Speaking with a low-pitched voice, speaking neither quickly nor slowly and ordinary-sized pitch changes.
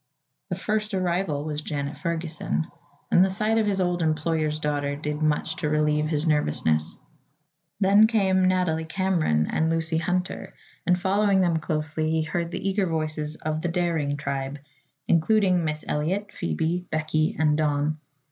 No: medium, 160 Hz; average, 155 wpm; average, 3.3 semitones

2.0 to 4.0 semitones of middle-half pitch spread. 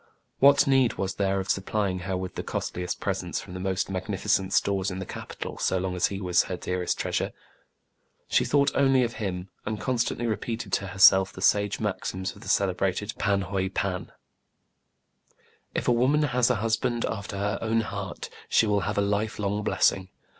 Yes: average, 2.9 semitones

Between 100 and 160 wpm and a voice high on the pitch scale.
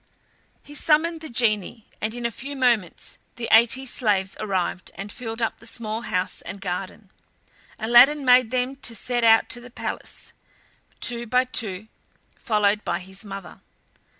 Yes: average, 155 wpm; high, 230 Hz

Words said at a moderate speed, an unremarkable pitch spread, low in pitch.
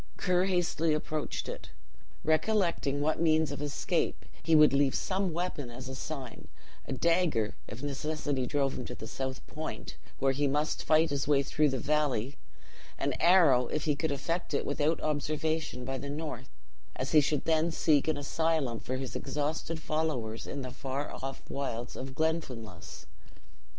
No: average, 160 wpm; average, 3.1 semitones; medium, 145 Hz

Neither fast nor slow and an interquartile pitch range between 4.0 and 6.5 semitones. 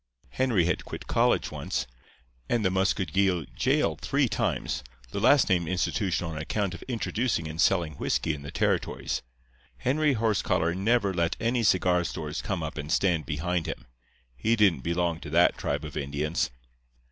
Yes: average, 160 wpm; average, 4.5 semitones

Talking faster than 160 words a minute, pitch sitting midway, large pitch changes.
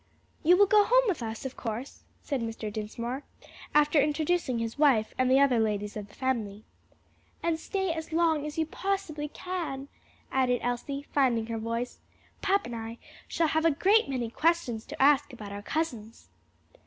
No: average, 175 wpm; very high, 270 Hz; wide, 5.8 semitones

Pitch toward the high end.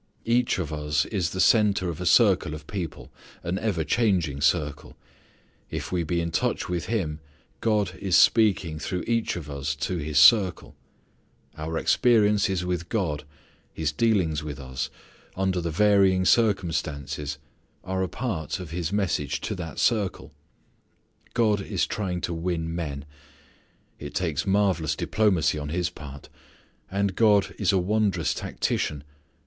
No: very low, 90 Hz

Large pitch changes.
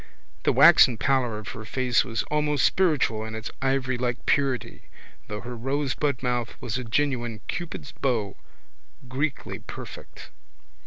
No: average, 3.3 semitones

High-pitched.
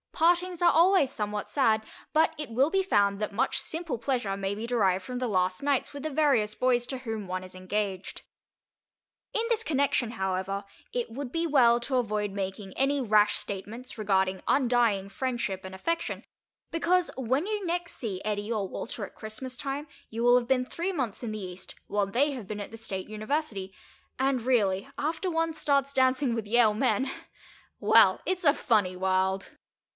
Yes: high, 235 Hz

